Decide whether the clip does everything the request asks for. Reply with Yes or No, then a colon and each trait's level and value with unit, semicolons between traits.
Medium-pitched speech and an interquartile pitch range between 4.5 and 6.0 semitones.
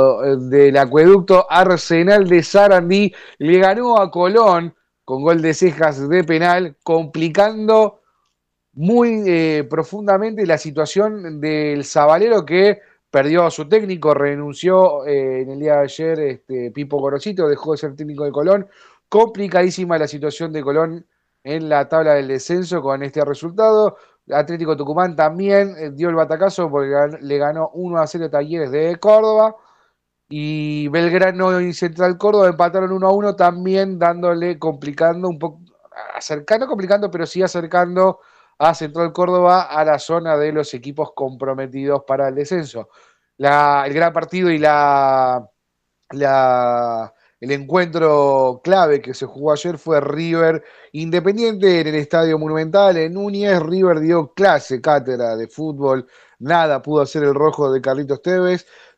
No: medium, 160 Hz; average, 4.0 semitones